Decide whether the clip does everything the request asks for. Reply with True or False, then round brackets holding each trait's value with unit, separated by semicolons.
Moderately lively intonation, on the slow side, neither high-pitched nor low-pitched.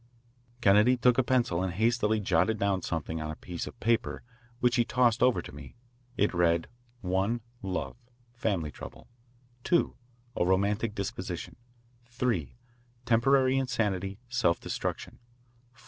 False (4.6 semitones; 125 wpm; 110 Hz)